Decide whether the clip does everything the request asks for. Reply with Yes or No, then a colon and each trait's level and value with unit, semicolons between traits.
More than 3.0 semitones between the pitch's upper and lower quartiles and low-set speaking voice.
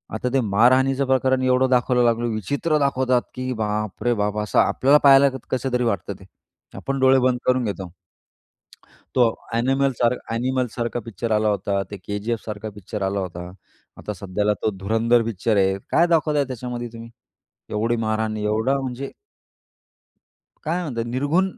Yes: average, 3.7 semitones; low, 120 Hz